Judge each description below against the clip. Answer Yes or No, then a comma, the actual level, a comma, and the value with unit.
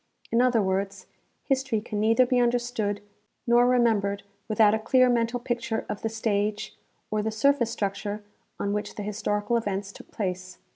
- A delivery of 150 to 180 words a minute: Yes, average, 160 wpm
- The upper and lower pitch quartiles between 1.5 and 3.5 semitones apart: Yes, average, 2.7 semitones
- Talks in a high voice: Yes, high, 220 Hz